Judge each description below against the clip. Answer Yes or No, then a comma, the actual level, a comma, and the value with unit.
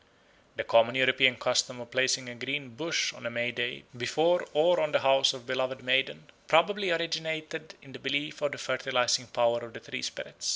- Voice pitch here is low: Yes, low, 130 Hz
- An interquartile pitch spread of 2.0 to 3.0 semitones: No, average, 3.9 semitones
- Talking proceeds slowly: No, average, 195 wpm